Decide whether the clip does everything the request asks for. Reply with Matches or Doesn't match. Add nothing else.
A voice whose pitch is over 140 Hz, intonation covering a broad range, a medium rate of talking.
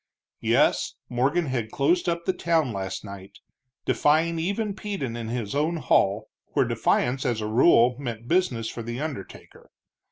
Doesn't match